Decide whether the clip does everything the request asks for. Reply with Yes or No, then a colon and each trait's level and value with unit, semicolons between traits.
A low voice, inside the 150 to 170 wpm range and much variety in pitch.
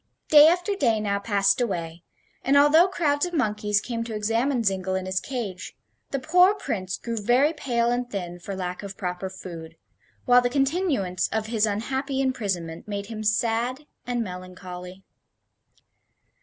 No: high, 220 Hz; average, 155 wpm; wide, 5.8 semitones